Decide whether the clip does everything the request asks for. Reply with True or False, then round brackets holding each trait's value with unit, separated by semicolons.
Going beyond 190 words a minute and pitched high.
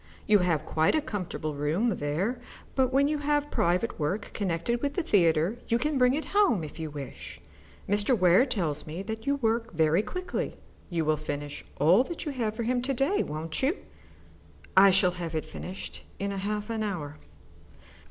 False (185 wpm; 200 Hz)